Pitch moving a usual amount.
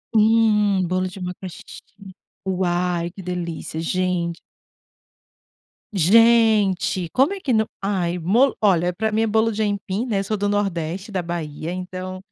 Yes: average, 3.2 semitones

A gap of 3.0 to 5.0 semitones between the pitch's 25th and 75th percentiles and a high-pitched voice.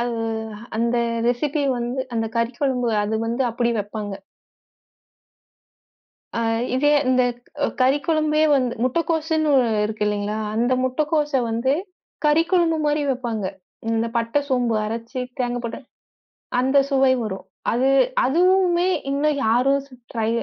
Yes: average, 4.1 semitones; very high, 255 Hz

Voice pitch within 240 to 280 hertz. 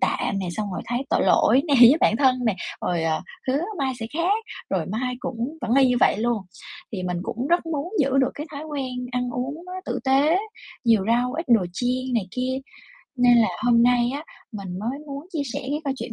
Yes: very high, 250 Hz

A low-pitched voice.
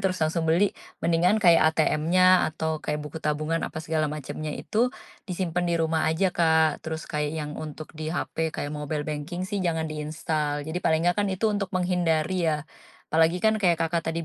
No: medium, 160 Hz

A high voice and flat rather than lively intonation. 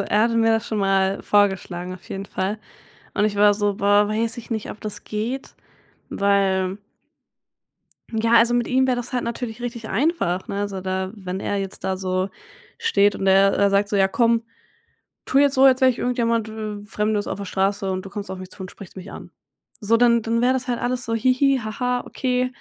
No: high, 210 Hz; average, 3.4 semitones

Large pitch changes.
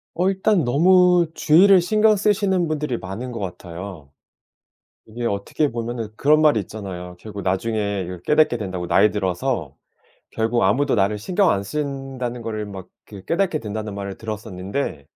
Yes: wide, 7.4 semitones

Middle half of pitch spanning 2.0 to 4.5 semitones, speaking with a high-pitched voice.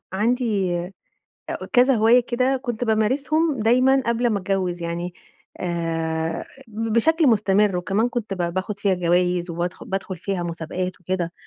No: average, 5.3 semitones; high, 195 Hz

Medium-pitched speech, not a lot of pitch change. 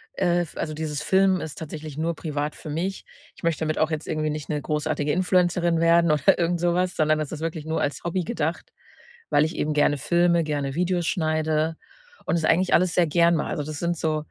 Yes: medium, 160 Hz; narrow, 2.0 semitones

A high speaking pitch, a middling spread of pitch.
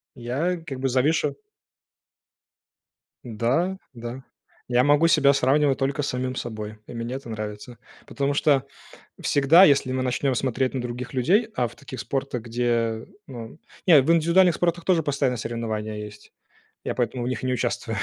No: low, 130 Hz; average, 3.3 semitones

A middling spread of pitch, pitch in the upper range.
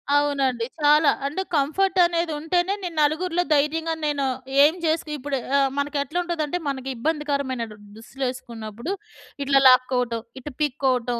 Yes: average, 3.5 semitones; very high, 290 Hz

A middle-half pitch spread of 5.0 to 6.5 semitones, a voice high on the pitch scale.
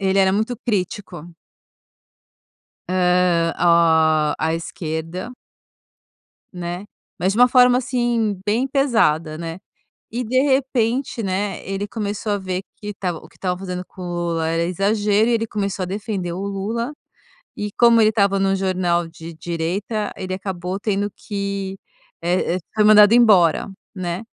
No: average, 3.5 semitones; high, 195 Hz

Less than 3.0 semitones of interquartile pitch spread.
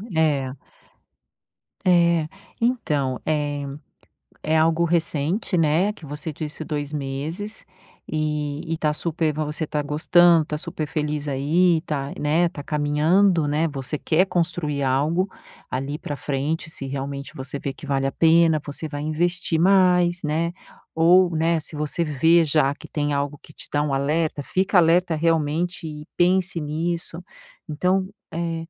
Yes: narrow, 2.5 semitones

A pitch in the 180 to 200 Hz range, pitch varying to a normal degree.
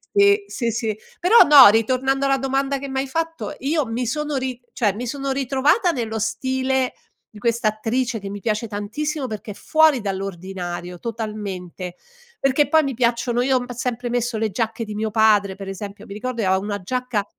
No: high, 235 Hz; average, 4.2 semitones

